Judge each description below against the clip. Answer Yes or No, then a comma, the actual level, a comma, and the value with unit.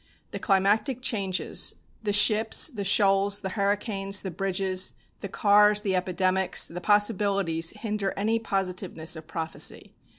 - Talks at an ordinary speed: No, slow, 130 wpm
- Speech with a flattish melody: Yes, narrow, 1.9 semitones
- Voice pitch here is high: Yes, high, 195 Hz